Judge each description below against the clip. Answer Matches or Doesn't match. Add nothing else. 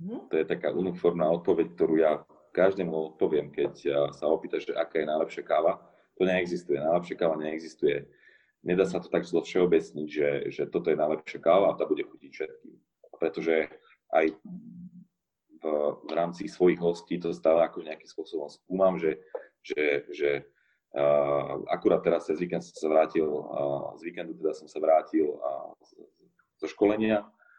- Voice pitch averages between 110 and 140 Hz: Doesn't match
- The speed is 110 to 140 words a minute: Doesn't match